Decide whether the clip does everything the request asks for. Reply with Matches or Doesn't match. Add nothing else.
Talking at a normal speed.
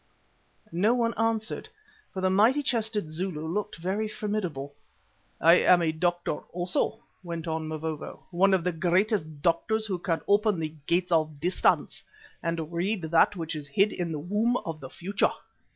Matches